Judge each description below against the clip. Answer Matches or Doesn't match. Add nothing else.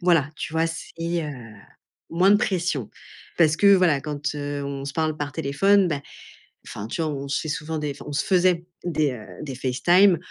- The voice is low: Doesn't match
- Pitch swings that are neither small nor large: Matches